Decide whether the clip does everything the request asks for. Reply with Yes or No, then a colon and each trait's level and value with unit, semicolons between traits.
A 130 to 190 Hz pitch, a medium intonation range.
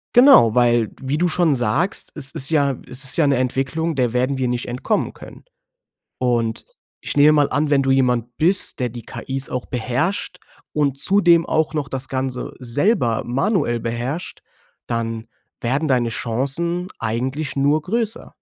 Yes: low, 135 Hz; average, 4.3 semitones